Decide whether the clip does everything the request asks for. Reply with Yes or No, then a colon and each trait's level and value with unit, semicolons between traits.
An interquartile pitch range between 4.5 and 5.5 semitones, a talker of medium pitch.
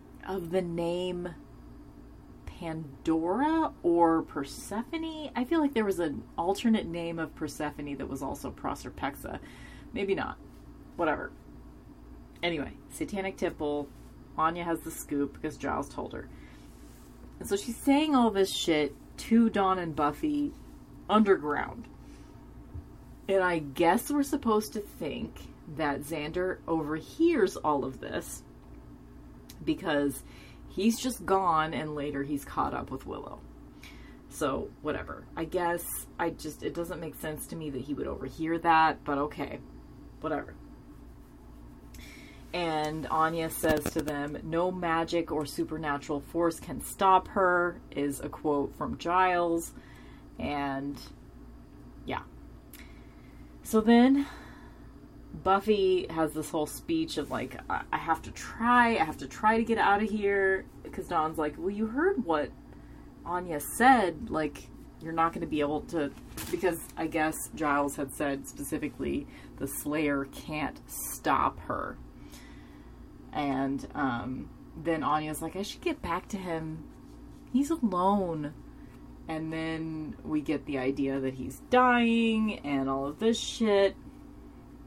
Yes: average, 5.2 semitones; medium, 160 Hz